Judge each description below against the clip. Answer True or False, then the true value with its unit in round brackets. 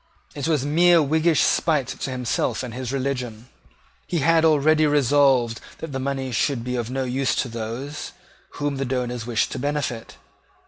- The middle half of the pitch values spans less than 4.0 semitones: True (3.1 semitones)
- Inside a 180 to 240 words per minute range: False (170 wpm)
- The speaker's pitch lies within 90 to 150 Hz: True (135 Hz)